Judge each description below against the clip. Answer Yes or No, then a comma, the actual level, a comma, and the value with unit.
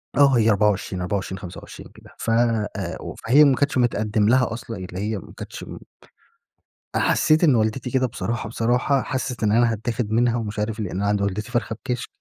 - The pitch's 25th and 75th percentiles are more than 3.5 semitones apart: No, average, 2.9 semitones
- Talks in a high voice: No, low, 115 Hz